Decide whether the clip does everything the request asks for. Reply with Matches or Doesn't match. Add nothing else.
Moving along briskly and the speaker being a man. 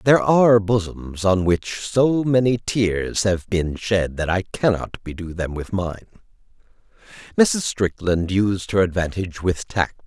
Doesn't match